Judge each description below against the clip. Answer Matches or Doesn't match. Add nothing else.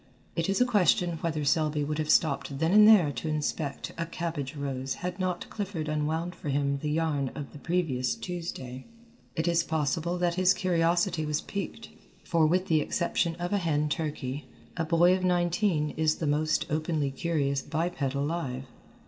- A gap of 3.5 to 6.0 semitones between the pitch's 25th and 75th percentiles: Doesn't match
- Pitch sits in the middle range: Matches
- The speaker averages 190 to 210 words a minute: Doesn't match